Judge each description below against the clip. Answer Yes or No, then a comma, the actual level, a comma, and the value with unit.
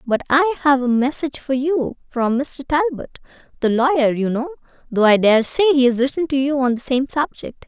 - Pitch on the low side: No, very high, 270 Hz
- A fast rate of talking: Yes, fast, 210 wpm